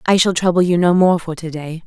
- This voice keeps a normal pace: No, fast, 290 wpm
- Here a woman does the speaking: Yes, female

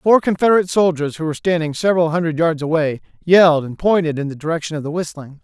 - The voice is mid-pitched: Yes, medium, 165 Hz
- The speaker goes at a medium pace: No, fast, 210 wpm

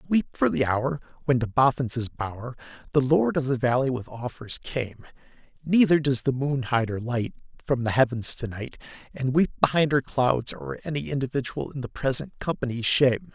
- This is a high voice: No, low, 130 Hz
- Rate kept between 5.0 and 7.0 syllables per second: Yes, 5.3 syllables/s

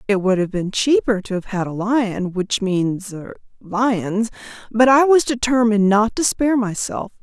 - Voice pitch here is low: No, high, 215 Hz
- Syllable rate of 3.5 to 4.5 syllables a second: Yes, 4.4 syllables/s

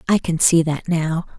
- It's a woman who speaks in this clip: Yes, female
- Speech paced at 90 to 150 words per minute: No, fast, 215 wpm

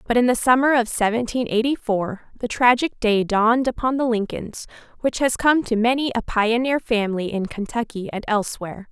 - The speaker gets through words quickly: No, average, 180 wpm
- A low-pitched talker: No, high, 230 Hz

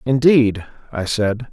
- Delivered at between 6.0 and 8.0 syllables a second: No, 3.5 syllables/s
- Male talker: Yes, male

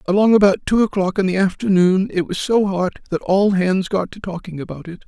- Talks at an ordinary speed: No, fast, 225 wpm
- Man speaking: Yes, male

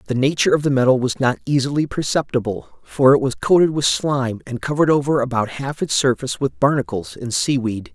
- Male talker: Yes, male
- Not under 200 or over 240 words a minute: Yes, fast, 205 wpm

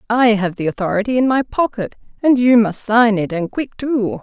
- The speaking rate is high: Yes, fast, 215 wpm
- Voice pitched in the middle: No, high, 225 Hz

